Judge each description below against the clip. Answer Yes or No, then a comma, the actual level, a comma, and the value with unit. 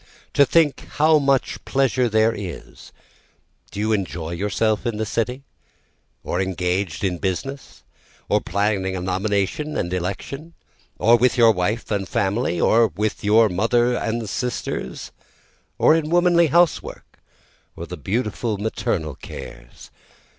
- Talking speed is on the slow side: Yes, slow, 130 wpm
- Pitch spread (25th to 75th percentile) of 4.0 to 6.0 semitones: Yes, average, 4.8 semitones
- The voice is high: No, low, 110 Hz